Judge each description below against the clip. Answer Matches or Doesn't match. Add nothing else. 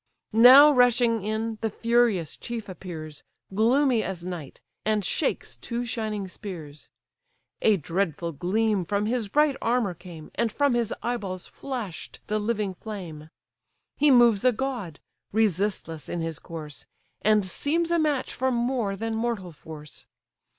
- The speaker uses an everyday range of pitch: Matches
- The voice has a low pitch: Doesn't match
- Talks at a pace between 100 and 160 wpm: Matches